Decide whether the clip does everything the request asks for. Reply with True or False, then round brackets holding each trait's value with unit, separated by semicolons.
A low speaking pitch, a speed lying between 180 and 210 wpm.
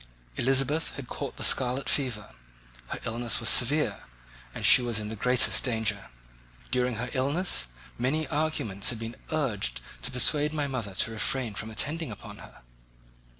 False (125 Hz; 155 wpm)